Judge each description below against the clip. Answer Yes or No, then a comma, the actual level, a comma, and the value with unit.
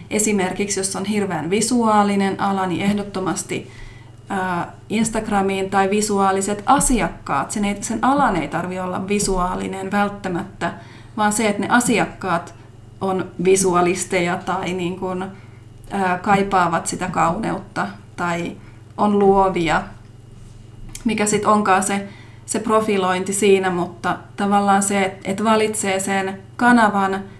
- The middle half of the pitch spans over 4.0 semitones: No, narrow, 2.4 semitones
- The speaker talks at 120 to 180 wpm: No, average, 105 wpm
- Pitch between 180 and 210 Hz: Yes, high, 190 Hz